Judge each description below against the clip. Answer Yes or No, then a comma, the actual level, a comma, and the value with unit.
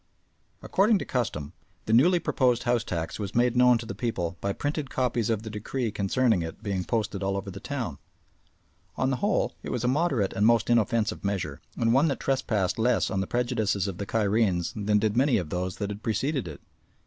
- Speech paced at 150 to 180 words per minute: No, fast, 205 wpm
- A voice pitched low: Yes, low, 110 Hz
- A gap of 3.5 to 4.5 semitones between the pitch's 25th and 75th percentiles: Yes, average, 4.1 semitones